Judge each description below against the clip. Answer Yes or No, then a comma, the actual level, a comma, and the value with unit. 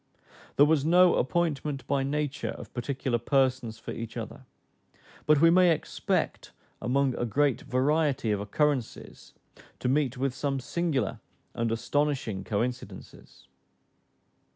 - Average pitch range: Yes, average, 3.6 semitones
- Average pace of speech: No, slow, 125 wpm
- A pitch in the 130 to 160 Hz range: Yes, low, 135 Hz